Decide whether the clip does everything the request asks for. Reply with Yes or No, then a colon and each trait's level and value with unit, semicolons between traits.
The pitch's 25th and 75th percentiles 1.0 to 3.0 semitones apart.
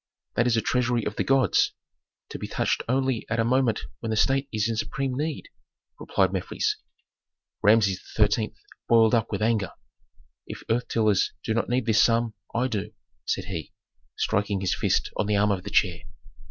Yes: average, 2.7 semitones